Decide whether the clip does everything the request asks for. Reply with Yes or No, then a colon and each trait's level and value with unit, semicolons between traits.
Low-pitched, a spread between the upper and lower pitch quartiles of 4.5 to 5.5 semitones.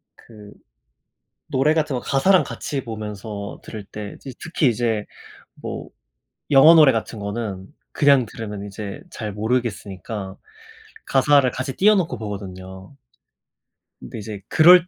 Yes: low, 115 Hz; average, 5.2 semitones